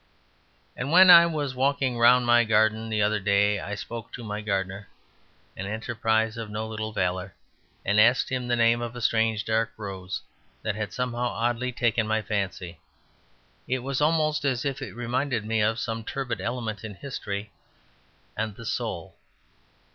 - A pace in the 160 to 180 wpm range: Yes, average, 170 wpm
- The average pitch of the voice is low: Yes, low, 110 Hz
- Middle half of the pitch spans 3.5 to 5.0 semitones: No, average, 2.7 semitones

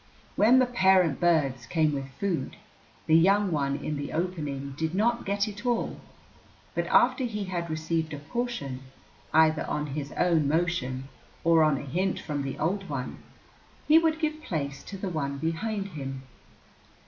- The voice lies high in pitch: No, medium, 165 Hz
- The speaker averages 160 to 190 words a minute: Yes, average, 165 wpm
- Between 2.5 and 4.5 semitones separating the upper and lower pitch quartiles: No, wide, 5.6 semitones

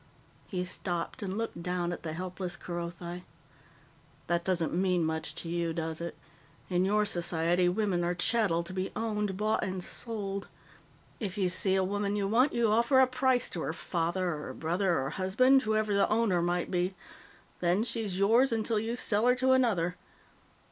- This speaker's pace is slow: No, average, 175 wpm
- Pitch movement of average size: Yes, average, 3.8 semitones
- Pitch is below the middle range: No, high, 190 Hz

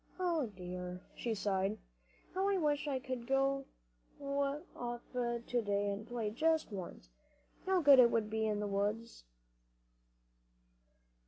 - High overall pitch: Yes, high, 235 Hz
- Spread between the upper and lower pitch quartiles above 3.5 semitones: Yes, average, 5.3 semitones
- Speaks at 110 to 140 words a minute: Yes, slow, 135 wpm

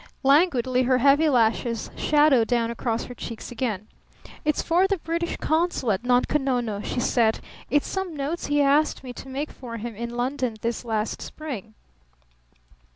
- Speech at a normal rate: Yes, average, 160 wpm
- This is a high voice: Yes, very high, 255 Hz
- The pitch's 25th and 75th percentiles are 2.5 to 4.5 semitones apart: Yes, average, 4.1 semitones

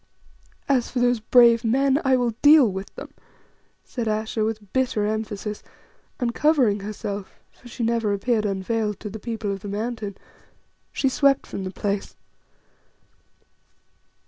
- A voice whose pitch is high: Yes, high, 225 Hz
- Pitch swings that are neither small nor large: Yes, average, 3.0 semitones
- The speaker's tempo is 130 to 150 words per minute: Yes, average, 145 wpm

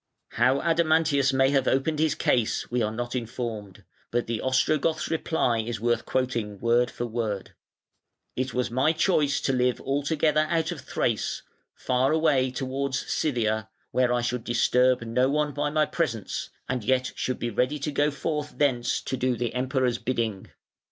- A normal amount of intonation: Yes, average, 3.5 semitones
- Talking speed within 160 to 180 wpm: Yes, average, 165 wpm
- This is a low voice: Yes, low, 130 Hz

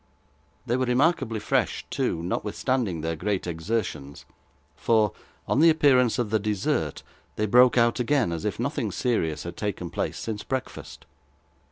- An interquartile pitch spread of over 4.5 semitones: Yes, wide, 5.5 semitones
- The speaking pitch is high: No, low, 110 Hz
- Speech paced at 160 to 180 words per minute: No, average, 150 wpm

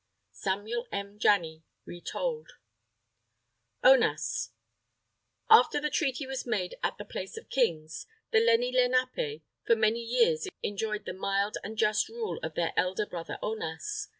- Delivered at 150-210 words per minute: No, slow, 135 wpm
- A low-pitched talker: No, high, 225 Hz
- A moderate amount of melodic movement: No, wide, 6.5 semitones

